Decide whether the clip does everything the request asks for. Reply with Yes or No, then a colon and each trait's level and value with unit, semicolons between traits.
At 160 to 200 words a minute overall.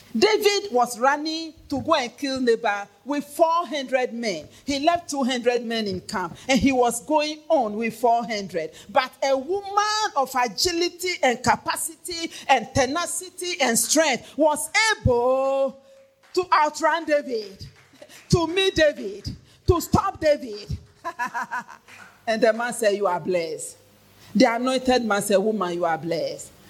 No: slow, 135 wpm